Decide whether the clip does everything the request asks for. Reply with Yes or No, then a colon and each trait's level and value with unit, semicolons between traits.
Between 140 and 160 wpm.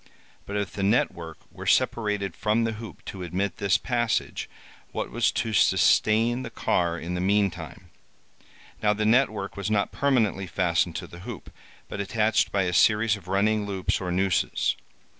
No: average, 175 wpm